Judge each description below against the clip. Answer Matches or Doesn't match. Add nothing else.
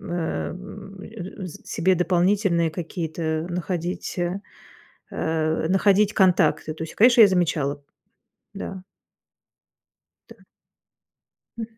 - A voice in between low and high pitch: Matches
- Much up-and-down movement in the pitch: Doesn't match